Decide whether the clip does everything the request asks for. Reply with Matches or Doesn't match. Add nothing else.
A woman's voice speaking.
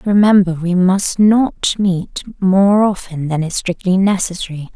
Matches